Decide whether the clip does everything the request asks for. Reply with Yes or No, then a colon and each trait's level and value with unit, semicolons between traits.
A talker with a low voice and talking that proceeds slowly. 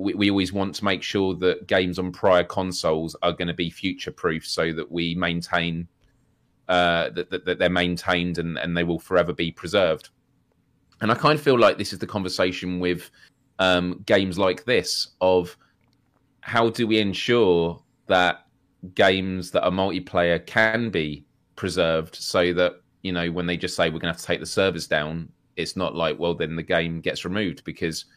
No: very low, 90 Hz; average, 185 wpm